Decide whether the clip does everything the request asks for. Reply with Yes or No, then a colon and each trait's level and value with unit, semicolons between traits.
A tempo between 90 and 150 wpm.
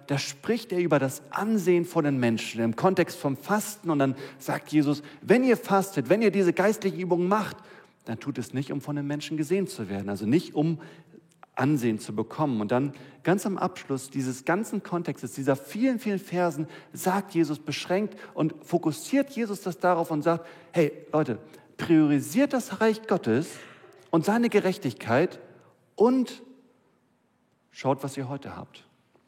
No: average, 165 wpm